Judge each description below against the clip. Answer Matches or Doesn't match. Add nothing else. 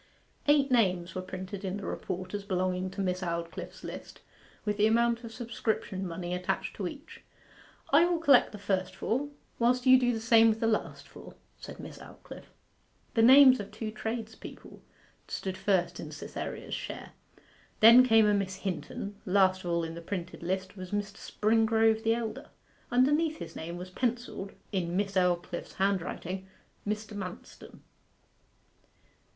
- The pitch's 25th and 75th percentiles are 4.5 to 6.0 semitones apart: Doesn't match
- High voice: Matches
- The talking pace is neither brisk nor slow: Matches